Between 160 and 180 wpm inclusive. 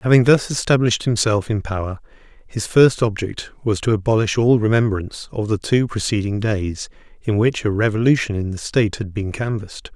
Yes: average, 175 wpm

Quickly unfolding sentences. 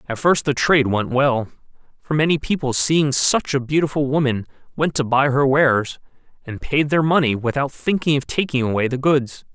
No: average, 190 wpm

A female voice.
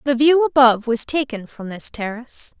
Yes: female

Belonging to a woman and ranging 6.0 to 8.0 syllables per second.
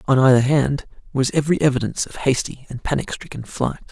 No: male; 6.1 syllables/s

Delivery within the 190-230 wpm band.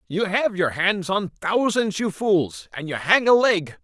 Yes: fast, 205 wpm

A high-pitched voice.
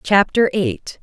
Yes: high, 200 Hz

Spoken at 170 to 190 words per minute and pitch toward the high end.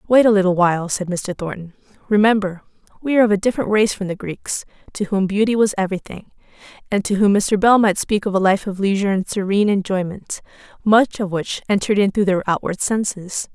No: fast, 205 wpm; high, 200 Hz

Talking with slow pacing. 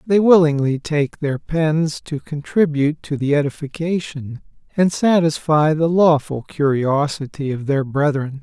Yes: slow, 130 wpm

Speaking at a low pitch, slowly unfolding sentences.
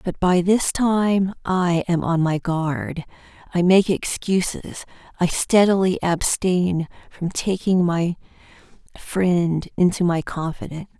No: medium, 180 Hz; slow, 120 wpm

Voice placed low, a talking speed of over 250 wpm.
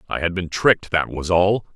No: very low, 90 Hz; fast, 240 wpm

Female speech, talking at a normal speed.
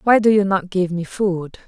No: female; fast, 250 wpm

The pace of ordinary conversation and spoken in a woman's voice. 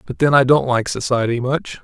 No: average, 195 wpm; male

